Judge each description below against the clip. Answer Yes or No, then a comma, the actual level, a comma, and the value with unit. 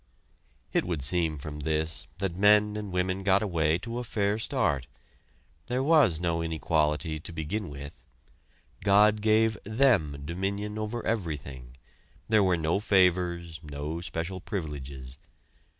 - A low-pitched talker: Yes, very low, 90 Hz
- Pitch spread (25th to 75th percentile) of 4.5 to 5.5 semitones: Yes, average, 5.1 semitones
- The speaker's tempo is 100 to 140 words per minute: Yes, slow, 135 wpm